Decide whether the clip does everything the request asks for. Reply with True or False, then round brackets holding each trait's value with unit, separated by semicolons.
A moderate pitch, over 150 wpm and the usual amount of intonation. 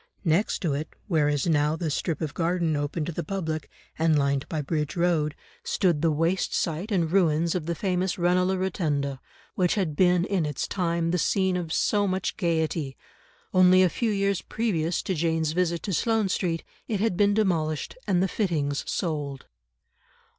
True (170 Hz; 180 wpm; 3.1 semitones)